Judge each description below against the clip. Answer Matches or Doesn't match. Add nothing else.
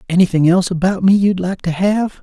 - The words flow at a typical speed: Doesn't match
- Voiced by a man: Matches